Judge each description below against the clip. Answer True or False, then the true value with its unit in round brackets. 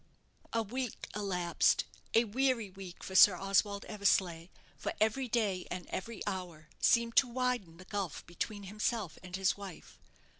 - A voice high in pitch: True (200 Hz)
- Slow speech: False (150 wpm)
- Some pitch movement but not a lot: True (3.8 semitones)